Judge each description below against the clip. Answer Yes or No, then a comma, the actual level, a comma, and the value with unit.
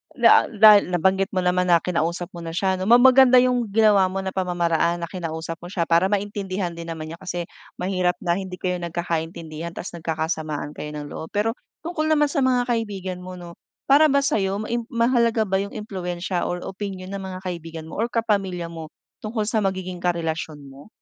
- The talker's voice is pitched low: No, medium, 185 Hz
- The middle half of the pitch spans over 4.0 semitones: No, average, 3.7 semitones